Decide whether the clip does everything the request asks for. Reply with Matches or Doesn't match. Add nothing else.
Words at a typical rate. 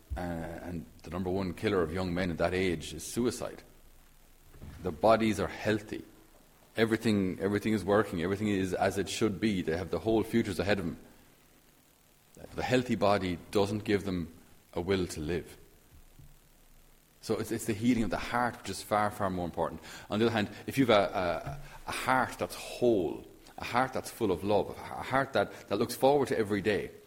Matches